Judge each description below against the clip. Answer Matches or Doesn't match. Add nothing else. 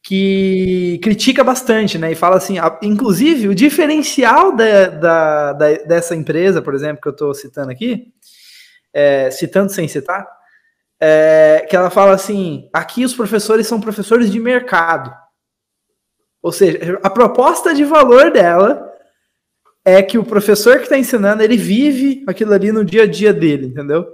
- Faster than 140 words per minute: Matches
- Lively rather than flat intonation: Matches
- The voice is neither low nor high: Doesn't match